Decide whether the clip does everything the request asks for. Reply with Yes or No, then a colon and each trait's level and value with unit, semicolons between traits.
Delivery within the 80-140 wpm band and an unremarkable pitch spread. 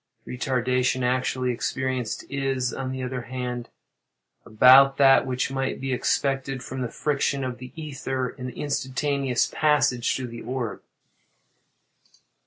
No: slow, 135 wpm; narrow, 1.2 semitones